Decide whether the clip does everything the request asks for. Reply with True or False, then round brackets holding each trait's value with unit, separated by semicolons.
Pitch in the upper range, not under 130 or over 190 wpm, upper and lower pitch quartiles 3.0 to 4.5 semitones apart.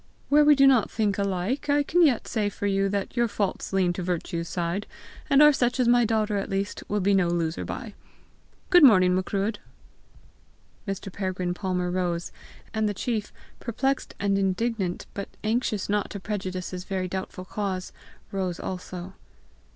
True (200 Hz; 170 wpm; 3.5 semitones)